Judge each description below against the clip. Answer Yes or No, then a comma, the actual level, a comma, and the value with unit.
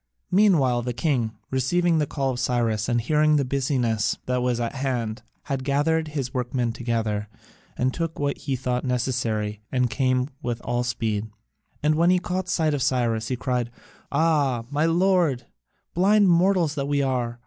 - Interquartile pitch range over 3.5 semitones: Yes, average, 4.1 semitones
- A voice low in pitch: Yes, low, 130 Hz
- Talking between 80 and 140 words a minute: No, average, 170 wpm